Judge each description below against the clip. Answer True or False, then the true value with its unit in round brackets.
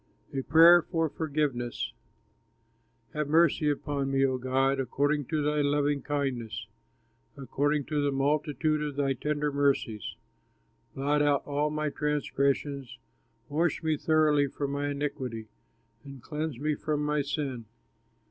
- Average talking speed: False (130 wpm)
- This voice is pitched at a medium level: True (145 Hz)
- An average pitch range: False (1.7 semitones)